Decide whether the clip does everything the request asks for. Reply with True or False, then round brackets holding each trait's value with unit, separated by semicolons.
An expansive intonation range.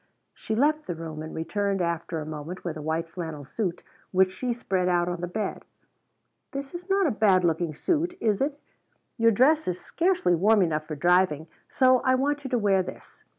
True (7.6 semitones)